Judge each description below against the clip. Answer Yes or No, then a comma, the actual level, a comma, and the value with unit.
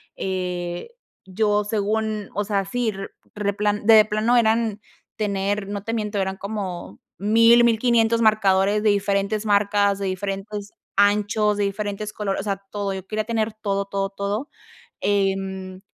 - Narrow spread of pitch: Yes, narrow, 1.6 semitones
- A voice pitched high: Yes, high, 205 Hz